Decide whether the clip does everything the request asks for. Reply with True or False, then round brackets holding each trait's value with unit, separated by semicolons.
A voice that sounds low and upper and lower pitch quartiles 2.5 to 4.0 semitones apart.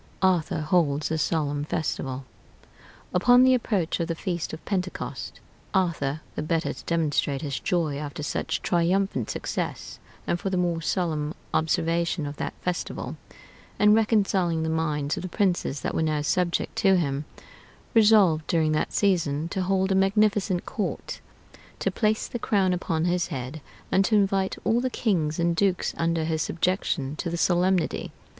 False (170 Hz; 3.6 semitones)